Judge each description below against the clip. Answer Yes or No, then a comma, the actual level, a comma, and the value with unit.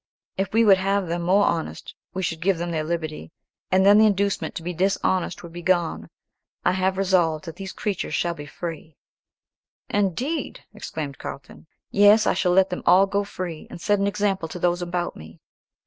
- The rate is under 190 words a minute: No, average, 195 wpm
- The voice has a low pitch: No, medium, 185 Hz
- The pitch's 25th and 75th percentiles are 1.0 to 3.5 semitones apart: Yes, average, 2.8 semitones